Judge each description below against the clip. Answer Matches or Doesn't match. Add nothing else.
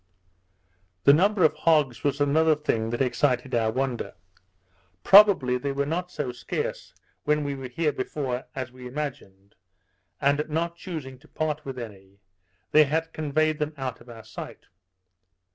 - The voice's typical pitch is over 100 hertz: Matches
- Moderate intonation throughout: Matches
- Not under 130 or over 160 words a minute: Matches